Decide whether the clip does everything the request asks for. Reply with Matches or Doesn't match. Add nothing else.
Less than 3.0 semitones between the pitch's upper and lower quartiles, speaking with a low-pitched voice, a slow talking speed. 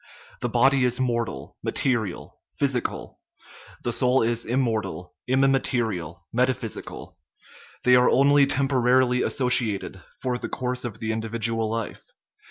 Matches